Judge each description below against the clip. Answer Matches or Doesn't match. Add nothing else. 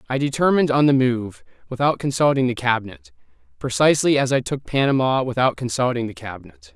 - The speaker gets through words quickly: Doesn't match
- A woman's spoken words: Doesn't match